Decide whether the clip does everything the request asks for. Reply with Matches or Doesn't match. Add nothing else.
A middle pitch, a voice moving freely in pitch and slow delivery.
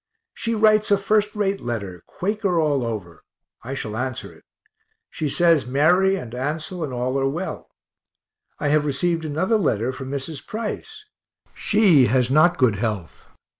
Doesn't match